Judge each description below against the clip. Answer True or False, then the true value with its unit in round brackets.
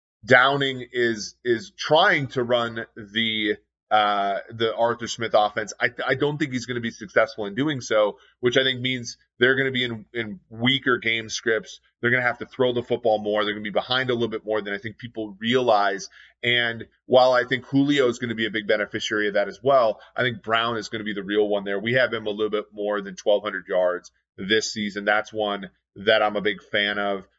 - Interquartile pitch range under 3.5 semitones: True (2.9 semitones)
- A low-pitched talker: True (115 Hz)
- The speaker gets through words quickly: True (235 wpm)